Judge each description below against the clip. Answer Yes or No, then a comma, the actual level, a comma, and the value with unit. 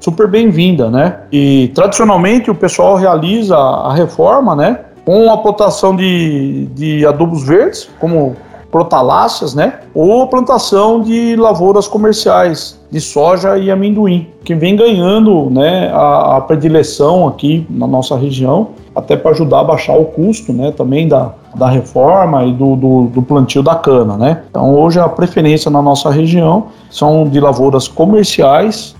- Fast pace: No, average, 150 wpm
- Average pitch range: No, wide, 6.1 semitones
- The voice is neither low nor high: Yes, medium, 165 Hz